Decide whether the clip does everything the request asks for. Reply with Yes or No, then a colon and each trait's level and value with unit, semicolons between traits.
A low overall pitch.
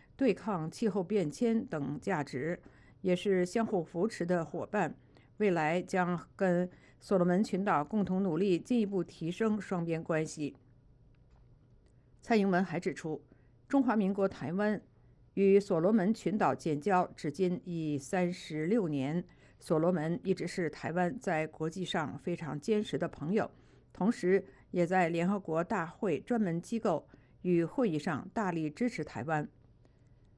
No: medium, 180 Hz